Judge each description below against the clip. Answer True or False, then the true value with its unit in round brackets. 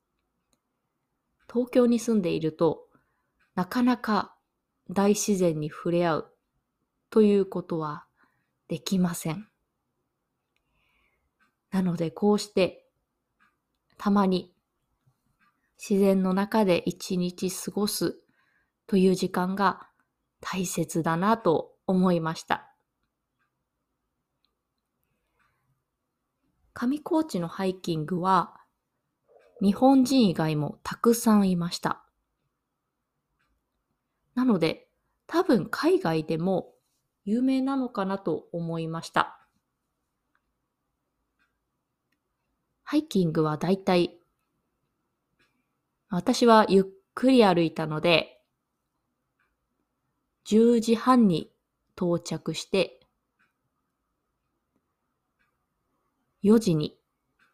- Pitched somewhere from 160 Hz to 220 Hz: True (190 Hz)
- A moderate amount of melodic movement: True (4.9 semitones)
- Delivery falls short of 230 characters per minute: True (150 characters per minute)